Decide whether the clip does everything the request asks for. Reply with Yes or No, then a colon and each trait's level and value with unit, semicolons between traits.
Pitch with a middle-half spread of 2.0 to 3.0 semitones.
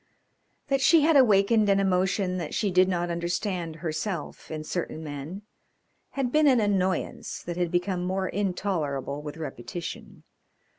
No: average, 3.6 semitones